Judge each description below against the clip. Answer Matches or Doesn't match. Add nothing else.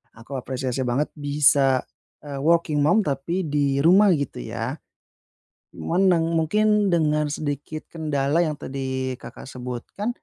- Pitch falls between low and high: Matches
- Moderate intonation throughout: Matches